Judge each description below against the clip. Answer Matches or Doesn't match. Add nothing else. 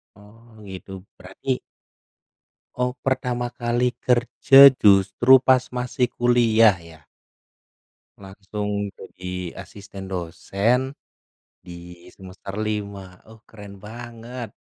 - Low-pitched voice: Matches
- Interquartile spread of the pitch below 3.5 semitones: Doesn't match